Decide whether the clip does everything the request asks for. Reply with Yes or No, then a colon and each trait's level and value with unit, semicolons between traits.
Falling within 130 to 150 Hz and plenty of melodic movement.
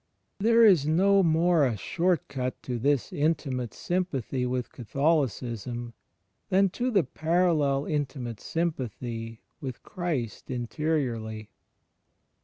Yes: medium, 140 Hz; wide, 5.7 semitones